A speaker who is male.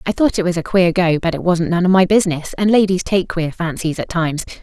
No: female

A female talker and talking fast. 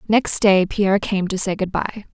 Yes: female; fast, 225 wpm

